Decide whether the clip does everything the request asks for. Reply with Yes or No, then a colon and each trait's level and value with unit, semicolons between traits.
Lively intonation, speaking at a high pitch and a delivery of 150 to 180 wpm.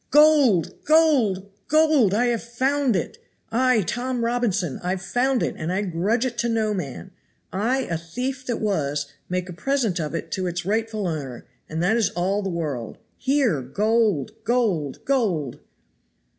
Yes: wide, 6.0 semitones; high, 210 Hz; average, 160 wpm